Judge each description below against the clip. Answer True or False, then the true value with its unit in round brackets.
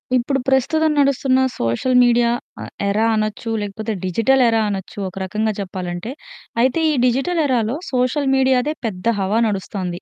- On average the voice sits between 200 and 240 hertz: True (230 Hz)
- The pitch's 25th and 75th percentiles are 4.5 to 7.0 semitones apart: True (4.8 semitones)